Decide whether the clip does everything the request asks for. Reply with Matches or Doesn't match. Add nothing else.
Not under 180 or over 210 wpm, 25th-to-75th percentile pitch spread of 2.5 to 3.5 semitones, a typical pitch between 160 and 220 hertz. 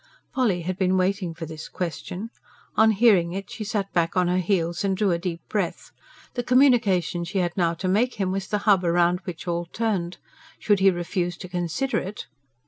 Matches